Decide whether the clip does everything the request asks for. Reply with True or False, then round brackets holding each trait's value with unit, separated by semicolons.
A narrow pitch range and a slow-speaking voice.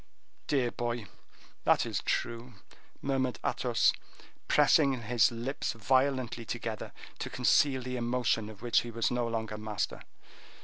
True (2.1 semitones; 130 wpm)